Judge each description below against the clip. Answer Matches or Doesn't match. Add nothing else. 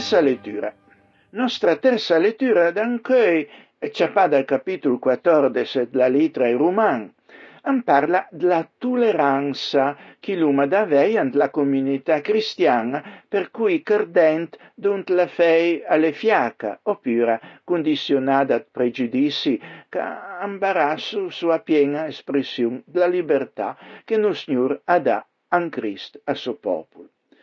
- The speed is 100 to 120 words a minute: Matches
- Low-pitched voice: Doesn't match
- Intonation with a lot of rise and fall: Matches